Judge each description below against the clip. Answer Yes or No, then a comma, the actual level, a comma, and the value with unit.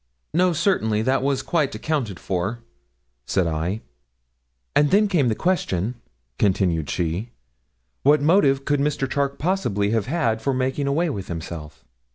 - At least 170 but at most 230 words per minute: No, average, 145 wpm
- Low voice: Yes, low, 130 Hz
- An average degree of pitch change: No, wide, 7.3 semitones